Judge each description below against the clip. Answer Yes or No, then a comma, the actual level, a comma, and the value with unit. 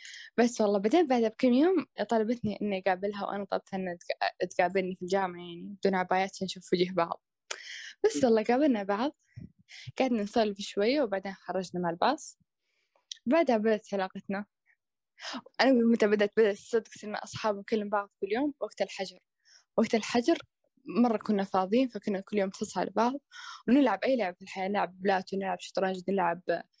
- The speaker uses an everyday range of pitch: Yes, average, 3.9 semitones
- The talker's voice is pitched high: Yes, high, 205 Hz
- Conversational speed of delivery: No, fast, 150 wpm